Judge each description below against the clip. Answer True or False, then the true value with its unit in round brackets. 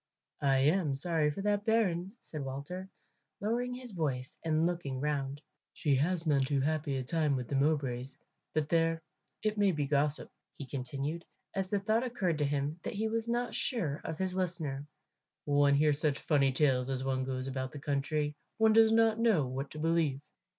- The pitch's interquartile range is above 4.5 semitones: True (5.2 semitones)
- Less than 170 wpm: False (185 wpm)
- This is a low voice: False (150 Hz)